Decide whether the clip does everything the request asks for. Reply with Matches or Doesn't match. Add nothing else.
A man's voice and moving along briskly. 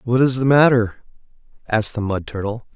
Doesn't match